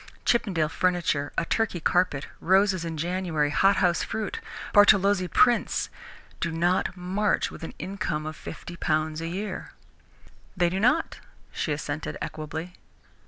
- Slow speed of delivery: Yes, slow, 130 wpm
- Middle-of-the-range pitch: Yes, medium, 175 Hz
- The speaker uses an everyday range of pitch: Yes, average, 3.5 semitones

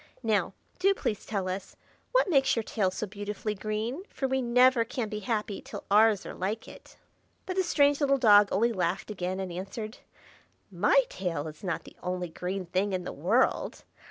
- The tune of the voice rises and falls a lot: No, average, 4.3 semitones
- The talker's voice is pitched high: Yes, high, 210 Hz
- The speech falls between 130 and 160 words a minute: No, average, 185 wpm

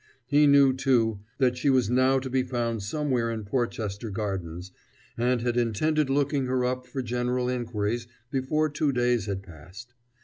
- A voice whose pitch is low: Yes, low, 125 Hz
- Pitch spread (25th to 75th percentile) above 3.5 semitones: No, average, 2.9 semitones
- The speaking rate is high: No, average, 165 wpm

